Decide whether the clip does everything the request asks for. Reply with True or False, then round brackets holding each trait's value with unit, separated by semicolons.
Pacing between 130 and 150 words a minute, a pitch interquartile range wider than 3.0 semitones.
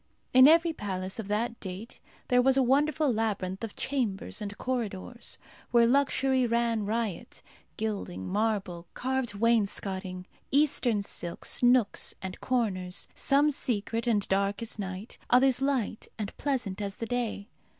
True (140 wpm; 4.2 semitones)